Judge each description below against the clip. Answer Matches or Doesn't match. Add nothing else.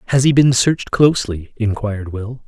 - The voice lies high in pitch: Doesn't match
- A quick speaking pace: Doesn't match